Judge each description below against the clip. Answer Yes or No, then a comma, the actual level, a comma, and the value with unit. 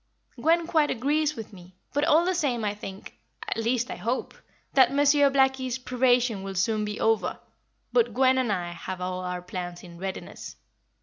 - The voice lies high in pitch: Yes, high, 235 Hz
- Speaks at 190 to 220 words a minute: No, average, 180 wpm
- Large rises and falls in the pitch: Yes, wide, 6.3 semitones